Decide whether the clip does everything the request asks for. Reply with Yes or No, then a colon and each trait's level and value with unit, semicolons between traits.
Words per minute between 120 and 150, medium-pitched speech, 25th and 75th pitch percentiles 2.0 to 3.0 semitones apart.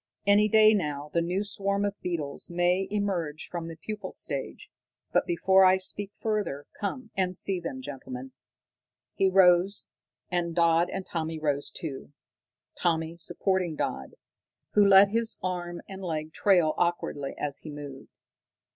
No: average, 145 wpm; medium, 180 Hz; average, 3.6 semitones